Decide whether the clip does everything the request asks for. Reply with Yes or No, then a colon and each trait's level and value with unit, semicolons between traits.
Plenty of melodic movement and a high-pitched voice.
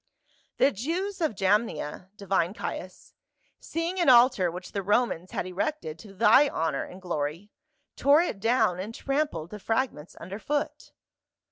Yes: wide, 7.1 semitones; high, 210 Hz